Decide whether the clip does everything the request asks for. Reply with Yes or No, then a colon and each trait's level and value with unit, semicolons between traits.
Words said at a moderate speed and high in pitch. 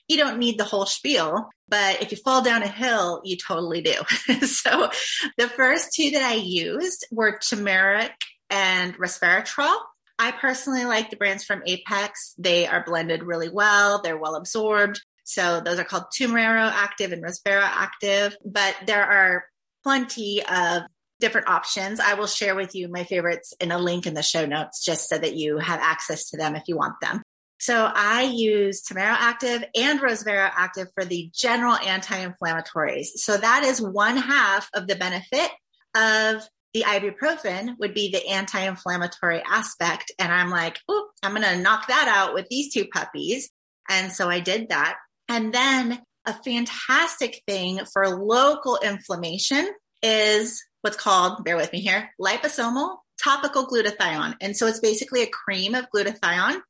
Yes: average, 165 wpm; high, 205 Hz